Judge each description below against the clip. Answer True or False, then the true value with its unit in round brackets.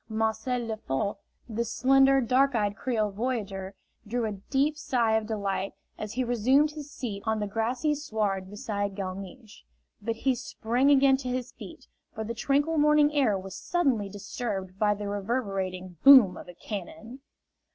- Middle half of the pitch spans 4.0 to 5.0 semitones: True (4.4 semitones)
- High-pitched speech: True (220 Hz)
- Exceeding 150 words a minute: True (160 wpm)